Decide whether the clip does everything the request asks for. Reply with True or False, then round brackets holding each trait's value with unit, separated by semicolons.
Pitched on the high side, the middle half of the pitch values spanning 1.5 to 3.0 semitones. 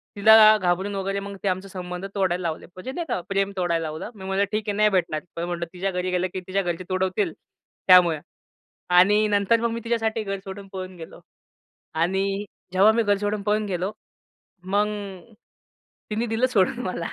True (195 Hz; 2.5 semitones)